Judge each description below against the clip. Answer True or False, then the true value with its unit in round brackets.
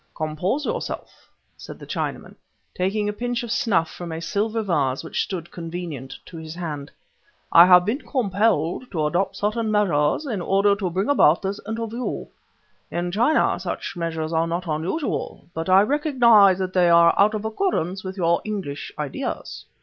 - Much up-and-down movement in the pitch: False (4.5 semitones)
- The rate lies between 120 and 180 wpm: True (165 wpm)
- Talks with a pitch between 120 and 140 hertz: False (185 Hz)